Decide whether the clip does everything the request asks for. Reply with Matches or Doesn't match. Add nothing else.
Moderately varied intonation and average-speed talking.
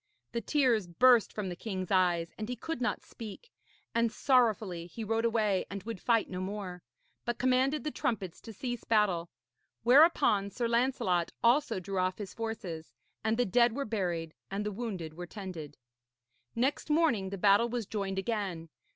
Matches